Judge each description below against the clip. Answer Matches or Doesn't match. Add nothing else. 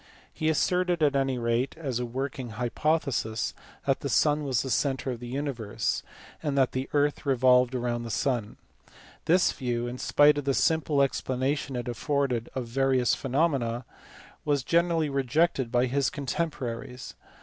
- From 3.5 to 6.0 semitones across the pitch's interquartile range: Doesn't match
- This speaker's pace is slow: Doesn't match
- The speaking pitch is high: Doesn't match